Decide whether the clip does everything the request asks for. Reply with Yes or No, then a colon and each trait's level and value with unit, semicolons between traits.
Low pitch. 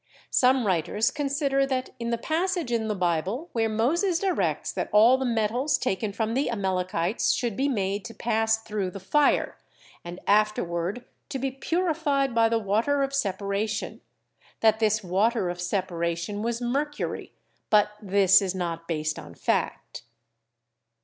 No: high, 220 Hz